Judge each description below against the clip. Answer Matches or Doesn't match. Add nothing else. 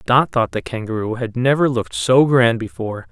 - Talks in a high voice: Doesn't match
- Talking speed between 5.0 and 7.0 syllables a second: Matches